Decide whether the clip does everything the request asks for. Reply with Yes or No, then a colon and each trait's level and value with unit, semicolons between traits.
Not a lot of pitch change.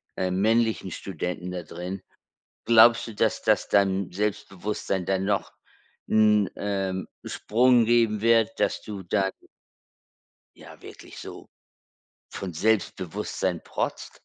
No: average, 3.0 semitones